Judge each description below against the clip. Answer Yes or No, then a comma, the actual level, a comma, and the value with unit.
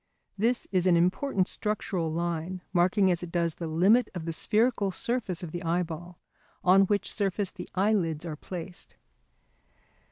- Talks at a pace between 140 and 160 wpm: Yes, average, 155 wpm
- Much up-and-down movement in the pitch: No, average, 3.0 semitones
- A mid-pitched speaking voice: Yes, medium, 180 Hz